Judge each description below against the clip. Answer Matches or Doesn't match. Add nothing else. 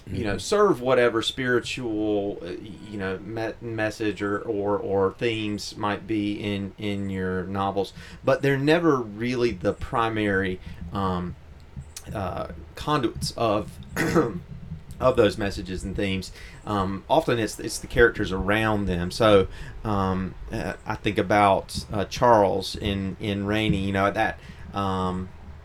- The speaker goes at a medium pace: Doesn't match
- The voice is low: Matches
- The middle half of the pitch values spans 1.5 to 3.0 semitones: Matches